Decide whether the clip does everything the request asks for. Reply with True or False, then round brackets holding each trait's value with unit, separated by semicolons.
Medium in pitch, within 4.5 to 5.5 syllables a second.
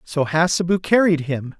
True (165 Hz; 4.7 syllables/s)